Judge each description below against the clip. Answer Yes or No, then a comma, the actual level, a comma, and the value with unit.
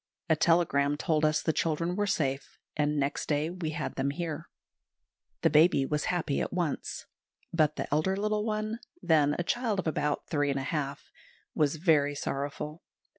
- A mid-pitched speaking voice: Yes, medium, 155 Hz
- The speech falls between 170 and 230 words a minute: Yes, average, 175 wpm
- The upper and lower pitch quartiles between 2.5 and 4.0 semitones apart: Yes, average, 3.2 semitones